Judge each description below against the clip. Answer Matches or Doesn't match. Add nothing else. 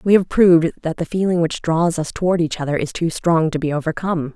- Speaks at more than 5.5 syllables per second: Matches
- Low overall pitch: Doesn't match